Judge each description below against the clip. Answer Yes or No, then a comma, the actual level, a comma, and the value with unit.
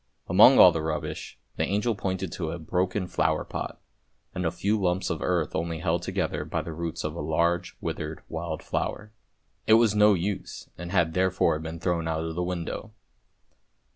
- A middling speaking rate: Yes, average, 190 wpm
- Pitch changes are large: No, narrow, 2.4 semitones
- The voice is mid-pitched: No, very low, 85 Hz